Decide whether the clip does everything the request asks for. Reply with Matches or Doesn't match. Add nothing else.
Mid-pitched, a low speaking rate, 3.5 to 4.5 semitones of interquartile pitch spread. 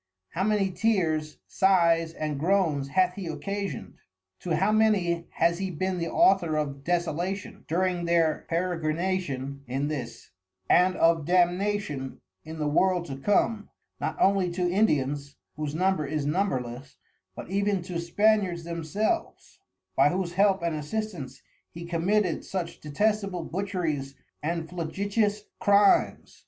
Matches